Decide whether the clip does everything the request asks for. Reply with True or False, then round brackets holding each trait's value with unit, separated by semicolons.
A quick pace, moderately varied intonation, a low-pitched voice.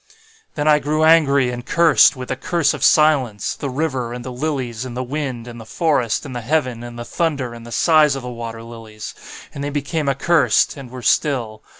True (215 wpm; 4.0 semitones; 130 Hz)